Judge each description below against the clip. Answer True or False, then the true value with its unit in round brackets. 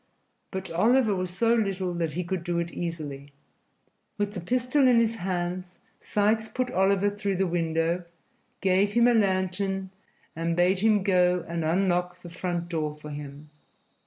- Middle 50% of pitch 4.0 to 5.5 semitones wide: False (3.2 semitones)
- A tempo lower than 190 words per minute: True (160 wpm)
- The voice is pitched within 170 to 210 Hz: True (185 Hz)